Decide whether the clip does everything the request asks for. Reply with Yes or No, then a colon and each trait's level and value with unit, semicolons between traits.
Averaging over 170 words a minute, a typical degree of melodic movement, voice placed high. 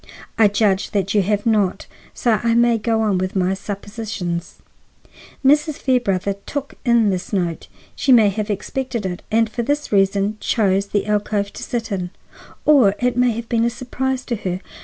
Yes: average, 180 wpm; average, 3.3 semitones; high, 215 Hz